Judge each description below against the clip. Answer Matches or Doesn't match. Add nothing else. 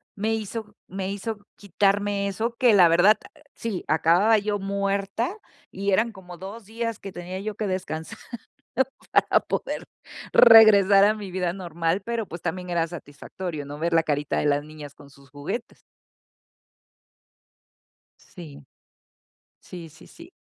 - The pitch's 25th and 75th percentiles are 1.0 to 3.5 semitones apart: Doesn't match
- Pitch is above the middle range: Matches